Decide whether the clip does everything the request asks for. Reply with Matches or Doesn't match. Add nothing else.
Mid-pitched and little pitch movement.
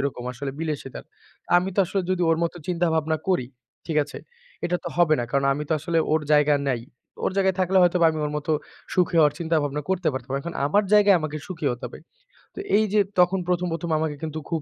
Doesn't match